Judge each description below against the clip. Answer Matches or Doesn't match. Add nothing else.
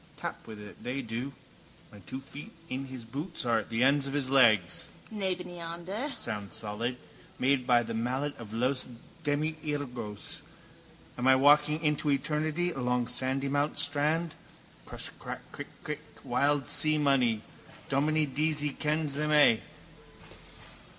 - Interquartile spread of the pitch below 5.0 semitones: Matches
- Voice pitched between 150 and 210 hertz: Doesn't match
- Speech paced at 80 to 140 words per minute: Matches